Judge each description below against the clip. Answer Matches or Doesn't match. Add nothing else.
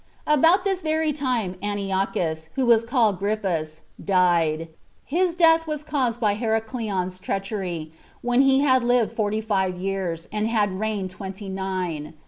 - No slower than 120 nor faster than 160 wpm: Matches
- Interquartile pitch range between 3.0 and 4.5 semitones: Doesn't match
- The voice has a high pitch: Matches